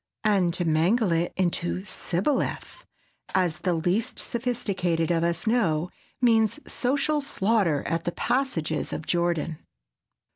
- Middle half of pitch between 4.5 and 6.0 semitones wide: Yes, wide, 5.6 semitones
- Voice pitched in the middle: Yes, medium, 180 Hz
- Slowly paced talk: Yes, slow, 110 wpm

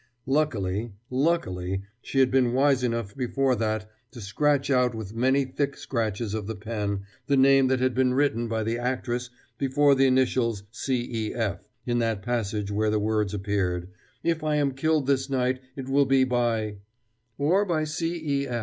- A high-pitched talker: No, low, 125 Hz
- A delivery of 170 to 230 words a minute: Yes, average, 175 wpm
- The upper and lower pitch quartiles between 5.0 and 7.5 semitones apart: No, average, 4.0 semitones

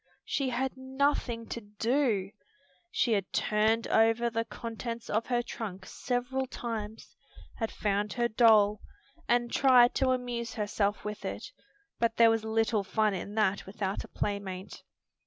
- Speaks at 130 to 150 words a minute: Yes, average, 145 wpm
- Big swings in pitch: No, narrow, 2.6 semitones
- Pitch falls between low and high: No, high, 225 Hz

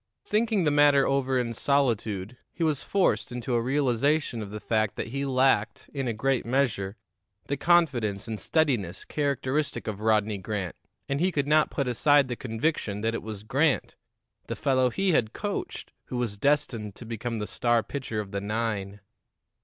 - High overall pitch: No, low, 125 Hz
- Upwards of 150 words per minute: Yes, average, 175 wpm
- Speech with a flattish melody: No, average, 4.7 semitones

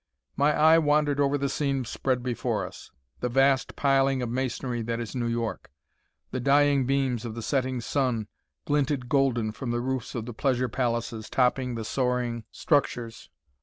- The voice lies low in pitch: Yes, low, 130 Hz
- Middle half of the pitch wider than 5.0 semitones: No, narrow, 2.6 semitones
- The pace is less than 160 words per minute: No, average, 165 wpm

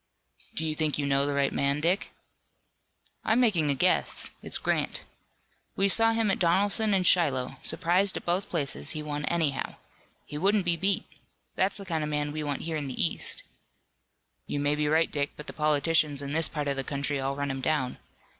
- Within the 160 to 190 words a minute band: No, average, 200 wpm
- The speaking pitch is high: No, medium, 150 Hz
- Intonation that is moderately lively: Yes, average, 3.9 semitones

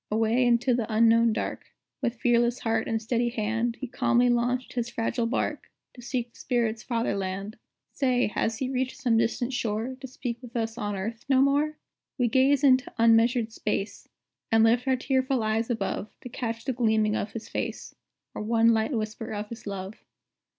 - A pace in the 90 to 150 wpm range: No, average, 185 wpm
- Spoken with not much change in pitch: Yes, narrow, 2.0 semitones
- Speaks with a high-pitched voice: Yes, high, 235 Hz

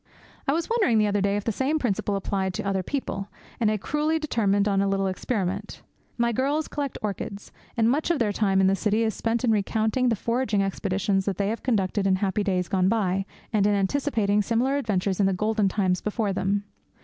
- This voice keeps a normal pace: No, fast, 215 wpm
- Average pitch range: Yes, average, 3.2 semitones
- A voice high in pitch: Yes, high, 205 Hz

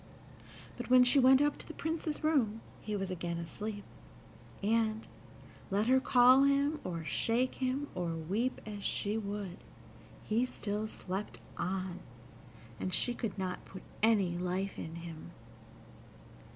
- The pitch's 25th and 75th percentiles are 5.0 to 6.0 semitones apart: Yes, wide, 5.5 semitones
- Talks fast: No, average, 140 wpm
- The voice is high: Yes, high, 210 Hz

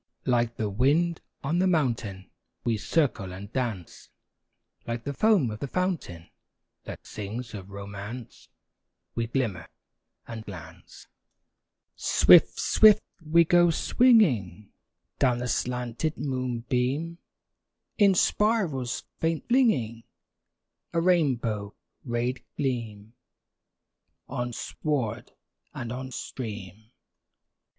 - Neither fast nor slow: No, slow, 100 wpm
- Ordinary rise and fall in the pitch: No, wide, 6.3 semitones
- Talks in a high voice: No, low, 125 Hz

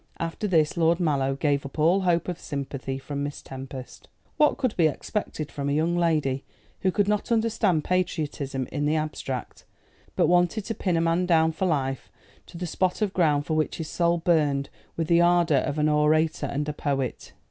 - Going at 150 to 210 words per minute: Yes, average, 195 wpm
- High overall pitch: No, medium, 160 Hz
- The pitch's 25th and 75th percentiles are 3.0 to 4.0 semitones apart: Yes, average, 3.5 semitones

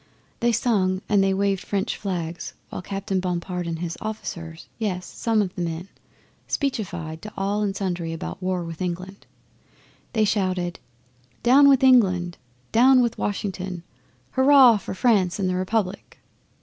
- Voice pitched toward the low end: No, high, 190 Hz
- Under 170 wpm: Yes, average, 150 wpm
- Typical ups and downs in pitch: Yes, average, 3.3 semitones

